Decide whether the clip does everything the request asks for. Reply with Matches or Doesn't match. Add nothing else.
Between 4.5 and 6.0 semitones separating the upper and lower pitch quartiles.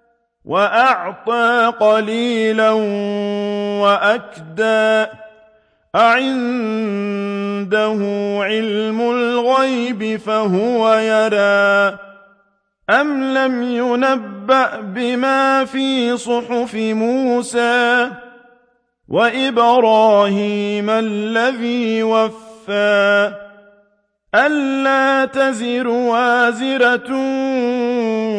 Doesn't match